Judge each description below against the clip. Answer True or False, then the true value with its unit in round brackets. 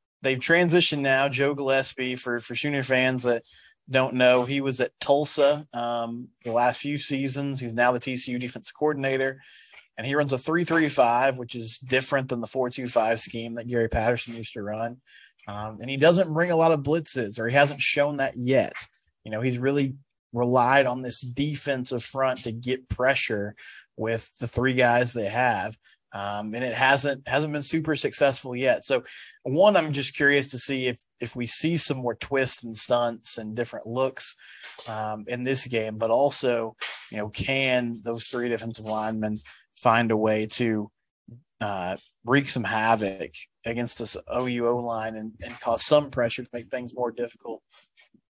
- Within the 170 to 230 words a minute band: True (175 wpm)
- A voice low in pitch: True (125 Hz)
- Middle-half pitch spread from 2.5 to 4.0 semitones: True (2.8 semitones)